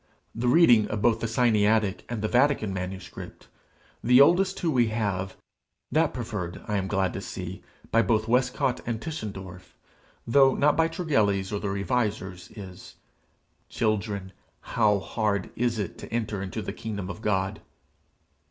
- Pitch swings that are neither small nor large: Yes, average, 3.9 semitones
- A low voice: Yes, low, 110 Hz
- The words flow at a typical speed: Yes, average, 150 wpm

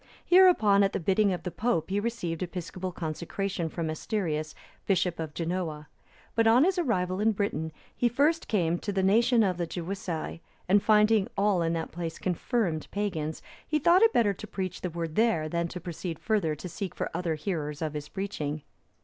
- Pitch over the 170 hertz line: Yes, medium, 185 Hz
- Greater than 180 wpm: Yes, average, 190 wpm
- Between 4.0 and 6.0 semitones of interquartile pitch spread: Yes, average, 4.3 semitones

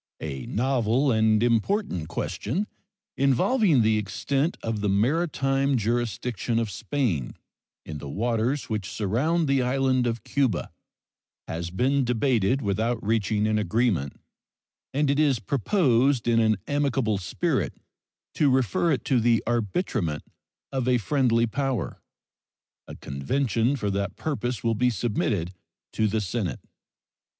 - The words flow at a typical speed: No, slow, 130 wpm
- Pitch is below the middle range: Yes, low, 120 Hz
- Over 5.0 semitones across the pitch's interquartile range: No, average, 4.4 semitones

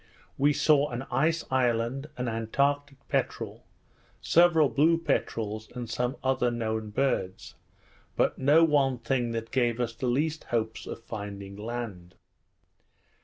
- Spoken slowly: Yes, slow, 130 wpm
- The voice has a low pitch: Yes, low, 125 Hz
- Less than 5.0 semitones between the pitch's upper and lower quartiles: Yes, average, 3.8 semitones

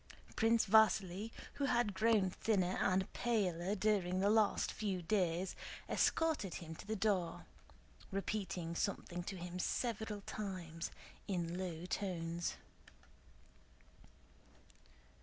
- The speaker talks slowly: Yes, slow, 105 wpm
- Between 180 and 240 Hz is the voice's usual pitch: Yes, high, 190 Hz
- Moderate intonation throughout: Yes, average, 3.4 semitones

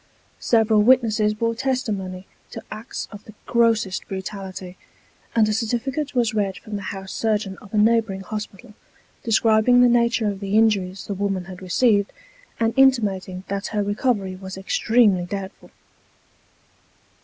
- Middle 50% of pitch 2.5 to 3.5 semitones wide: Yes, average, 3.0 semitones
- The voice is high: Yes, high, 210 Hz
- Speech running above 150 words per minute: No, average, 145 wpm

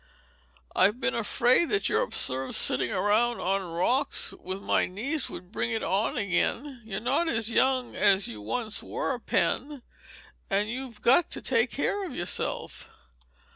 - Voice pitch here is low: No, high, 230 Hz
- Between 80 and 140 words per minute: No, average, 155 wpm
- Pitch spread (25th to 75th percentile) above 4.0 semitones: Yes, average, 5.0 semitones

